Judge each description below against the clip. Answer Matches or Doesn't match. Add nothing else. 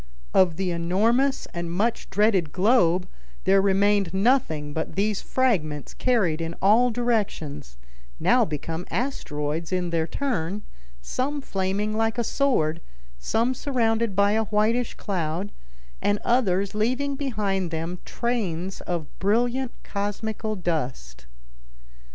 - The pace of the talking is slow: Matches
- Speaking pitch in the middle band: Doesn't match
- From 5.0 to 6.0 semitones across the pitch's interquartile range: Matches